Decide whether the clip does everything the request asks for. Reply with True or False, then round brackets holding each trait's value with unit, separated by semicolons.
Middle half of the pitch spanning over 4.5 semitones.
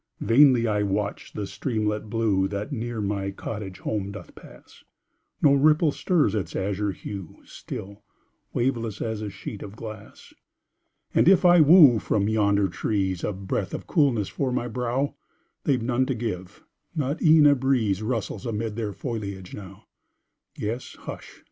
False (4.1 semitones)